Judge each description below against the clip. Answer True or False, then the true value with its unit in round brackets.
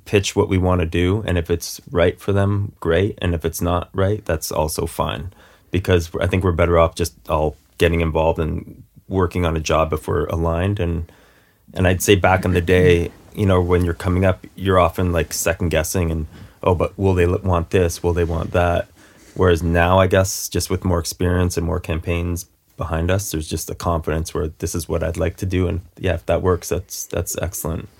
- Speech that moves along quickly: True (220 wpm)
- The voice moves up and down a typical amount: False (2.0 semitones)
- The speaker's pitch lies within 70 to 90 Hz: True (85 Hz)